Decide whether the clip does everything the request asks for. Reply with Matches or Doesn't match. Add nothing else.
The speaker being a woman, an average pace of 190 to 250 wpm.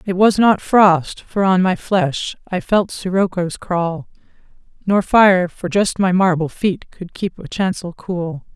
Doesn't match